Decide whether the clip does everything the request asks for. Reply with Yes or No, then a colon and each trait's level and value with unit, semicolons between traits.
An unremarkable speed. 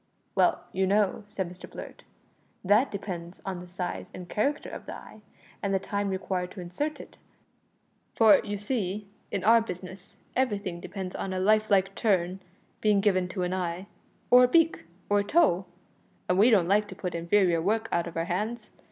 Yes: average, 185 wpm